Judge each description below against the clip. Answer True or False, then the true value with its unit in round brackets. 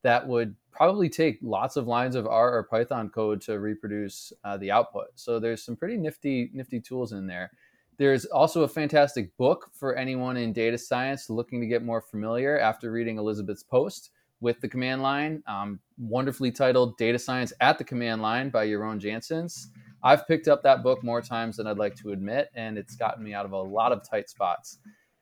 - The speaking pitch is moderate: False (120 Hz)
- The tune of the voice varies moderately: True (3.2 semitones)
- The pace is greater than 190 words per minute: True (200 wpm)